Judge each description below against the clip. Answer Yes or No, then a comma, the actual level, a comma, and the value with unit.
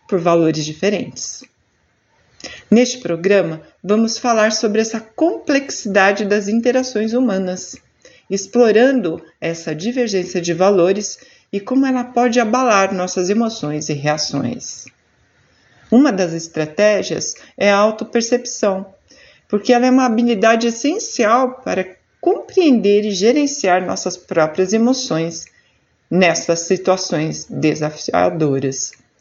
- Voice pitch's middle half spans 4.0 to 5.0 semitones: No, wide, 5.5 semitones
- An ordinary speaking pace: No, slow, 100 wpm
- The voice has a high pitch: Yes, high, 205 Hz